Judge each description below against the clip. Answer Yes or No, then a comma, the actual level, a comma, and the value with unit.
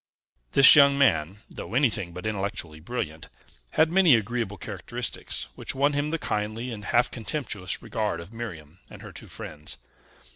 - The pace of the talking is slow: No, average, 155 wpm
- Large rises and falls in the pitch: Yes, wide, 6.3 semitones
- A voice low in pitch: Yes, low, 110 Hz